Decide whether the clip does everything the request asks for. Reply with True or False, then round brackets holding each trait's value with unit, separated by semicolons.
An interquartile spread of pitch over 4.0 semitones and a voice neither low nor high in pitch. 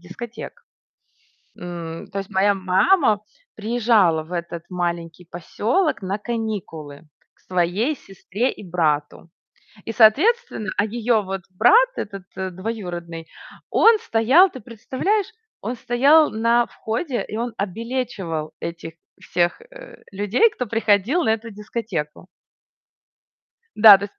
False (5.2 semitones; 210 Hz)